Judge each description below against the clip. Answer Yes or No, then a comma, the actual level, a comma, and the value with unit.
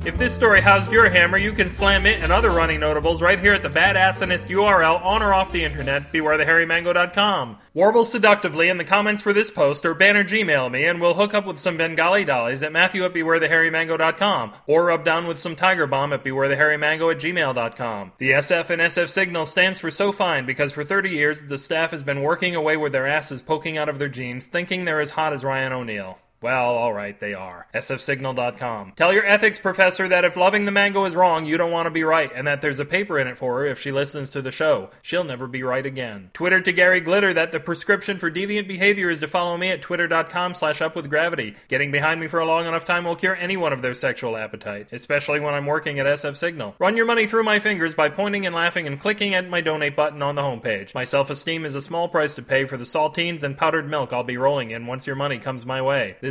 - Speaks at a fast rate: Yes, fast, 235 wpm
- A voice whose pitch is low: No, medium, 160 Hz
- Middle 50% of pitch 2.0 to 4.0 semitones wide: No, average, 4.6 semitones